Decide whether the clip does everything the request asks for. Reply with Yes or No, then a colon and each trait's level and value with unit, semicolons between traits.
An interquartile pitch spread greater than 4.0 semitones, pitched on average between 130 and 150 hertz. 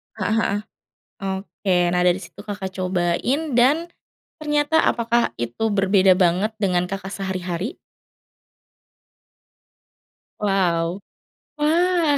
No: average, 4.7 semitones; high, 195 Hz